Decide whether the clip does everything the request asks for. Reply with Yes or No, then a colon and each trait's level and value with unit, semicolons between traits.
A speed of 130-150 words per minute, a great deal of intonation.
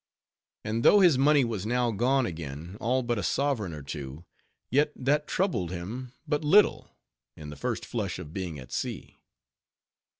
No: average, 165 wpm; wide, 8.4 semitones